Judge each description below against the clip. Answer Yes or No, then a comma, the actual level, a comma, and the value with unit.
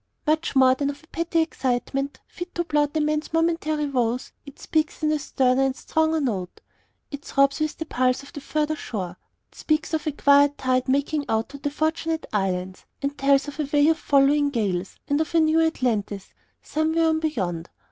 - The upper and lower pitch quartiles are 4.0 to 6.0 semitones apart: No, average, 3.4 semitones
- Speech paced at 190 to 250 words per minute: Yes, average, 200 wpm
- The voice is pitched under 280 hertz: No, very high, 285 Hz